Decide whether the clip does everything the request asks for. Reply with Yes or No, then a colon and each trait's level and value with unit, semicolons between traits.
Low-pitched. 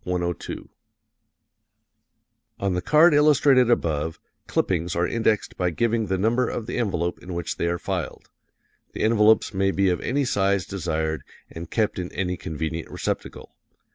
Yes: very low, 95 Hz